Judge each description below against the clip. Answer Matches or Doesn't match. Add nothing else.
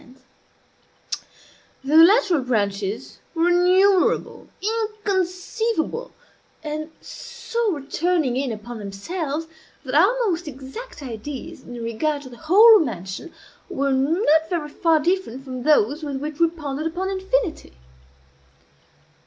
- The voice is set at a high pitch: Matches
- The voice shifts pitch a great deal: Matches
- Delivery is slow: Matches